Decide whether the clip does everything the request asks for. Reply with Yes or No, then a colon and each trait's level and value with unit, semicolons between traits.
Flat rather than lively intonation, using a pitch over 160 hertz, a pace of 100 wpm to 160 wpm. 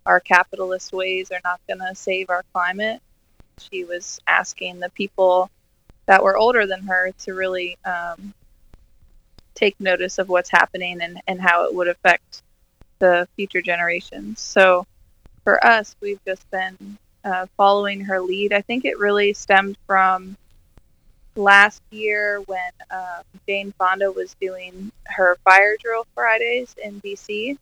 Yes: narrow, 2.1 semitones; high, 190 Hz; average, 145 wpm